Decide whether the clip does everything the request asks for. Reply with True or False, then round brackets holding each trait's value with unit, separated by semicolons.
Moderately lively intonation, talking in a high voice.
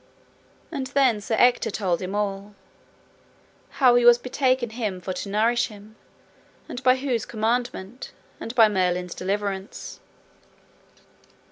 True (3.9 semitones; 220 Hz)